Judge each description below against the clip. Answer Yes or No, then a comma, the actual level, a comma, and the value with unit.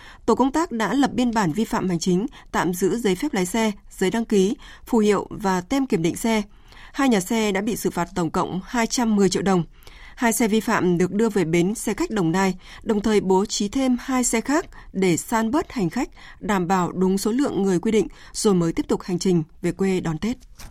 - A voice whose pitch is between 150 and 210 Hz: Yes, high, 205 Hz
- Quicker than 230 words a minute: Yes, average, 240 wpm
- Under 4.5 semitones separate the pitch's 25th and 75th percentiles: Yes, average, 3.8 semitones